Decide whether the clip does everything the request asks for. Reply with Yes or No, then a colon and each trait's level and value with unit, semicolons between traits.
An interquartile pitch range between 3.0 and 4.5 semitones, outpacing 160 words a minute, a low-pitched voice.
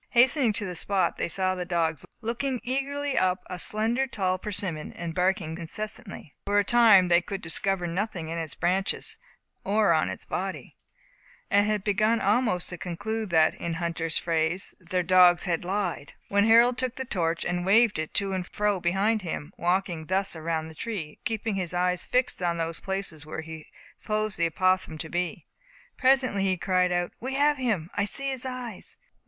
No: average, 3.9 semitones; average, 180 wpm; medium, 185 Hz